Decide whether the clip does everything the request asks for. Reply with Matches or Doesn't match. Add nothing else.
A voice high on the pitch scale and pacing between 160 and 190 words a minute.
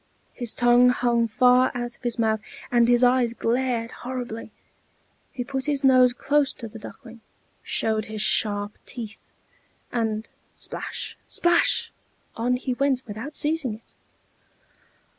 Doesn't match